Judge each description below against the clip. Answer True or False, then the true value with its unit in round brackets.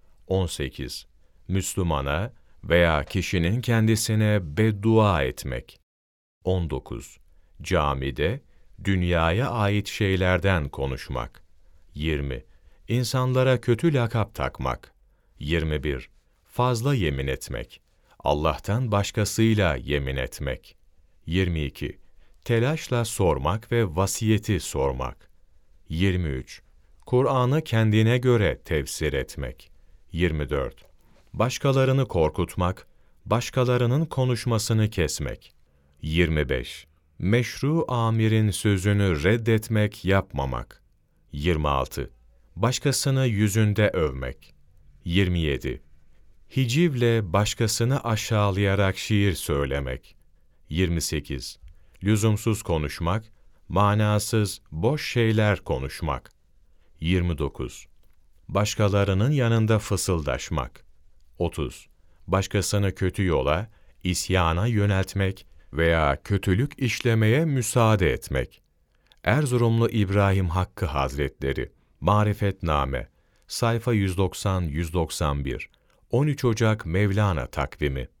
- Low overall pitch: True (95 Hz)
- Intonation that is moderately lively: False (6.5 semitones)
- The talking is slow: True (70 wpm)